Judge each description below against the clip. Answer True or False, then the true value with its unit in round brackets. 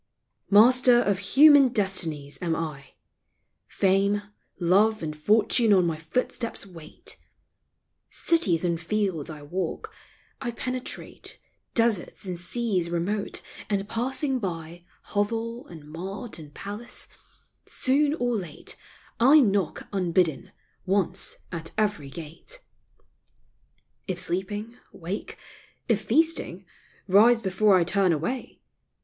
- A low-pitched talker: False (195 Hz)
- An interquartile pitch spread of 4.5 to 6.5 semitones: True (5.2 semitones)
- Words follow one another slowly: True (115 wpm)